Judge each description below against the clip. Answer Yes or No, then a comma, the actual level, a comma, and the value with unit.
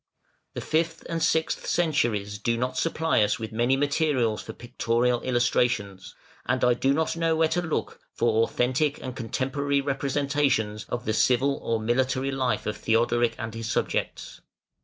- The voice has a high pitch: No, low, 125 Hz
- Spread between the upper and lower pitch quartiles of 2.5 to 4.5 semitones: Yes, average, 3.8 semitones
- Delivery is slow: No, average, 160 wpm